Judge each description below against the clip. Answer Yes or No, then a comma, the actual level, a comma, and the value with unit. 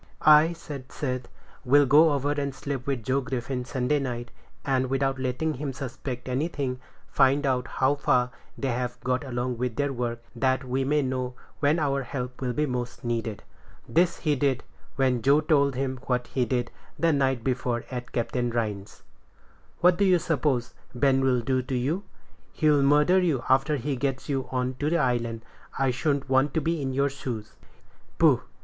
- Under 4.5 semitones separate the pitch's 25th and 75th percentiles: Yes, narrow, 2.4 semitones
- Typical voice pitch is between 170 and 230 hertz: No, low, 130 Hz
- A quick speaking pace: No, average, 175 wpm